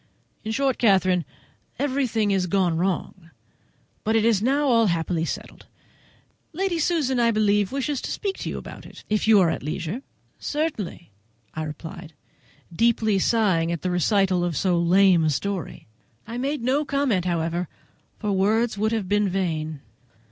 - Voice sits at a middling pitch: No, high, 200 Hz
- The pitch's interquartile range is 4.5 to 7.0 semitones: Yes, average, 5.1 semitones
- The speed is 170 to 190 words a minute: No, average, 160 wpm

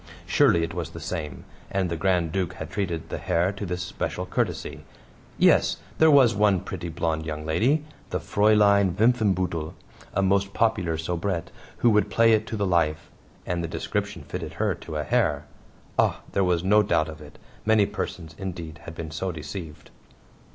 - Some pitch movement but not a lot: Yes, average, 3.8 semitones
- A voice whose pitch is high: No, very low, 90 Hz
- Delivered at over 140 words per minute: Yes, average, 180 wpm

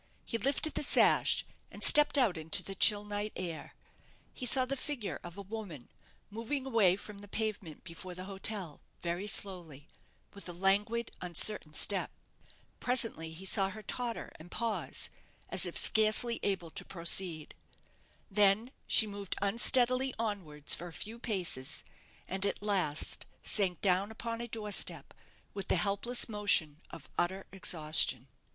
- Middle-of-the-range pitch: No, high, 200 Hz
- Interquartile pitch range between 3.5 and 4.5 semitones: Yes, average, 4.0 semitones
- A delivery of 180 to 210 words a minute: No, average, 155 wpm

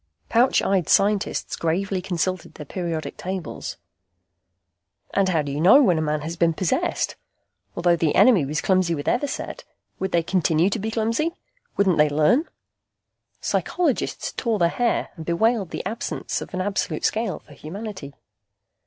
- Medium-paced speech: Yes, average, 155 wpm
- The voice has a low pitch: No, medium, 185 Hz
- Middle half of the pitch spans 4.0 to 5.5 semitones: Yes, average, 4.6 semitones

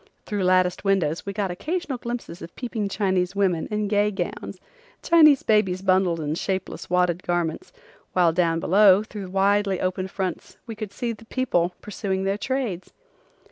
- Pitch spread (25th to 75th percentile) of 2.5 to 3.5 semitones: Yes, average, 2.8 semitones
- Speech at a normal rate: Yes, average, 155 wpm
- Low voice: No, high, 195 Hz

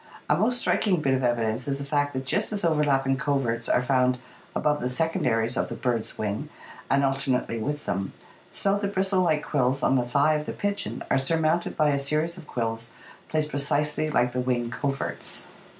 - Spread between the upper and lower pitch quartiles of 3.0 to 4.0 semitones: Yes, average, 3.6 semitones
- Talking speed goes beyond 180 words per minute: Yes, average, 195 wpm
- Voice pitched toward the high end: No, medium, 140 Hz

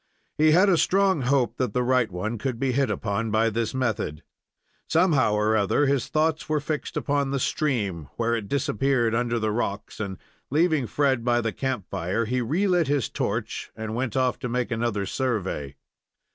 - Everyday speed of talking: Yes, average, 185 wpm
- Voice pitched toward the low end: Yes, low, 120 Hz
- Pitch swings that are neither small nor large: Yes, average, 4.3 semitones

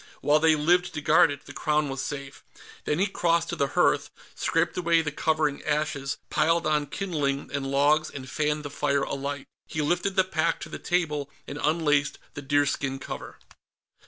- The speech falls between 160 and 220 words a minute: Yes, average, 185 wpm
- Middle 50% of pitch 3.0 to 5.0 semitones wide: No, narrow, 2.5 semitones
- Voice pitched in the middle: Yes, medium, 150 Hz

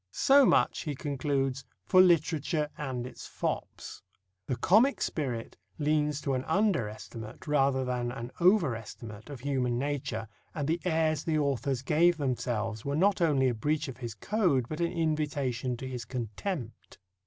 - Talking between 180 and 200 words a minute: No, average, 160 wpm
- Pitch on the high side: No, medium, 140 Hz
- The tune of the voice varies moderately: Yes, average, 4.2 semitones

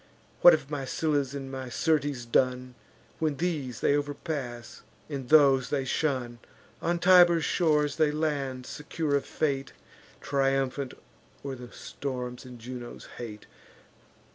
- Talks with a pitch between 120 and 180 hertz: Yes, medium, 140 Hz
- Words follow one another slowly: Yes, slow, 130 wpm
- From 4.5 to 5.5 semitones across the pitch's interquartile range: No, average, 3.0 semitones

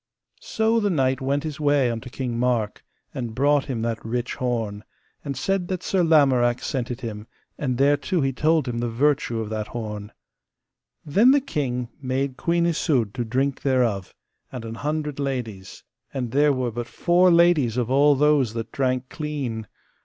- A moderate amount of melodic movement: Yes, average, 4.0 semitones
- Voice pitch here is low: Yes, low, 130 Hz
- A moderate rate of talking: Yes, average, 175 wpm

